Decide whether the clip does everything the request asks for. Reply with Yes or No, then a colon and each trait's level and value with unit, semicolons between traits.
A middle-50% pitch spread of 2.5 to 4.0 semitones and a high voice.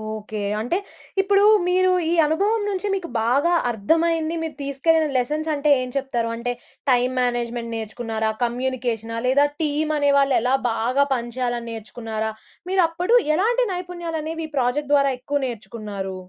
No: wide, 5.6 semitones; very high, 270 Hz